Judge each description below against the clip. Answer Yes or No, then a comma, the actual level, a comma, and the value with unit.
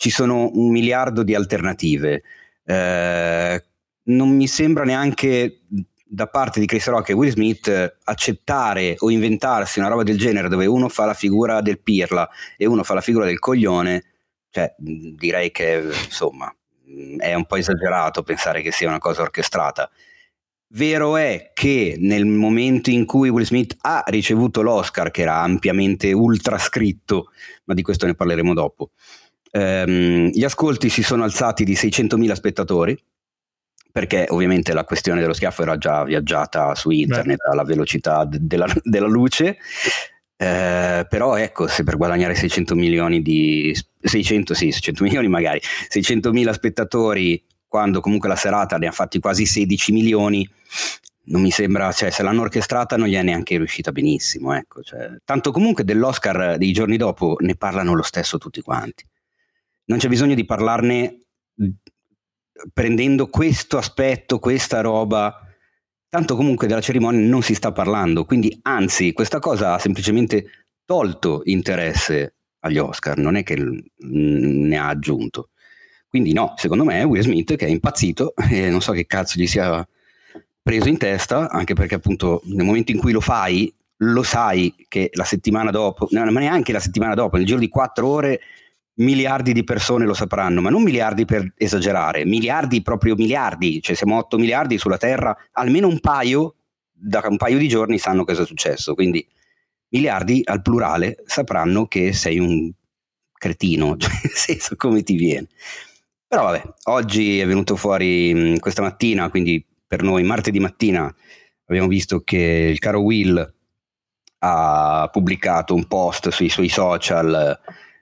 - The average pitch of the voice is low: Yes, low, 105 Hz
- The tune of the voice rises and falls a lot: No, average, 4.5 semitones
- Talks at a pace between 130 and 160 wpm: Yes, average, 155 wpm